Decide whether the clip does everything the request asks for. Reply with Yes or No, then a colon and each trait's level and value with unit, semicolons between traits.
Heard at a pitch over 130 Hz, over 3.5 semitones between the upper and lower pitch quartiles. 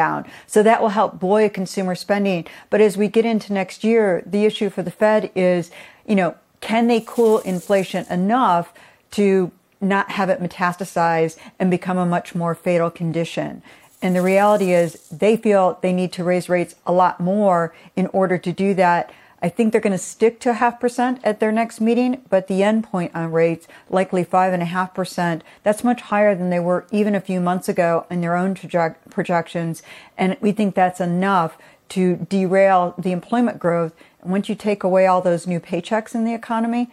No: high, 190 Hz; average, 3.2 semitones